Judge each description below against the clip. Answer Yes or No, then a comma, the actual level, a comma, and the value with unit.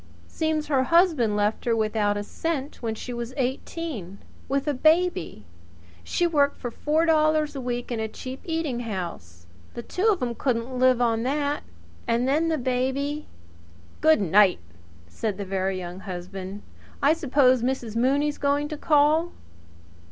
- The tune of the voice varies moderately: No, wide, 5.7 semitones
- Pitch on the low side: No, very high, 255 Hz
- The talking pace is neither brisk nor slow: Yes, average, 160 wpm